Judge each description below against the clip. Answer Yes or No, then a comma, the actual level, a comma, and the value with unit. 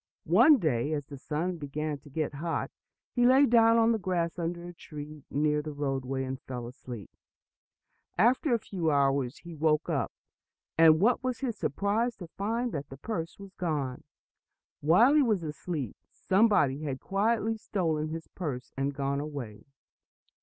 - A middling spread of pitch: No, wide, 6.4 semitones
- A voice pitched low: No, medium, 160 Hz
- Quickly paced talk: No, average, 165 wpm